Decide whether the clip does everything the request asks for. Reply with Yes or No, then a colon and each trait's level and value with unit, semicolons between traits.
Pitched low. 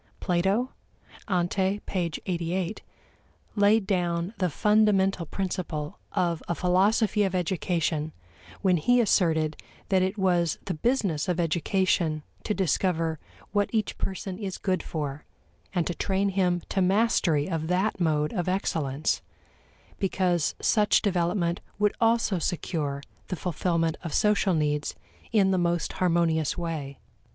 No: medium, 180 Hz